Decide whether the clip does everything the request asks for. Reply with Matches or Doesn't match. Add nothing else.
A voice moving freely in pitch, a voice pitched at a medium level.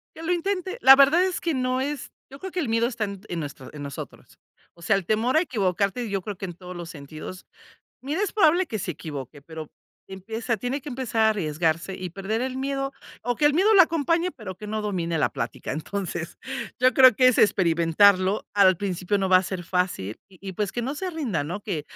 Doesn't match